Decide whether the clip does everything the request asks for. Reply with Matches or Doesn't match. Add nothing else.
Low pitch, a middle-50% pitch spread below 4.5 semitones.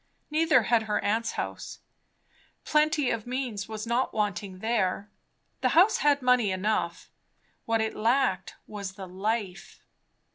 Doesn't match